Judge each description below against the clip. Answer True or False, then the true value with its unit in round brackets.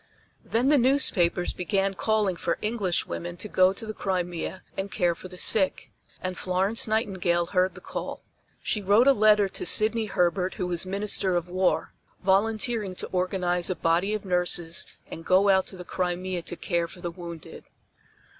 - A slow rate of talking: False (175 wpm)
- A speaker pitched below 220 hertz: True (185 Hz)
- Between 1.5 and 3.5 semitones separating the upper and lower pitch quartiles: True (2.9 semitones)